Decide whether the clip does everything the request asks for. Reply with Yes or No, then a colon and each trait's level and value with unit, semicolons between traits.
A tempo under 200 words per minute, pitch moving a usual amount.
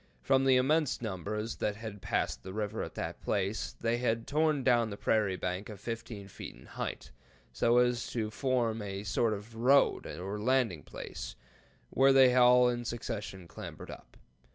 Yes: average, 175 wpm; average, 3.4 semitones